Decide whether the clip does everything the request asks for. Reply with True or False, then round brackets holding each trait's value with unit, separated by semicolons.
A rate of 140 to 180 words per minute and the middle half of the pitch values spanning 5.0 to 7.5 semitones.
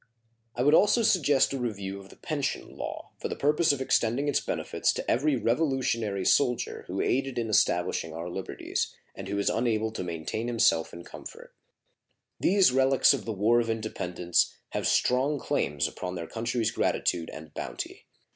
True (170 wpm; 5.6 semitones)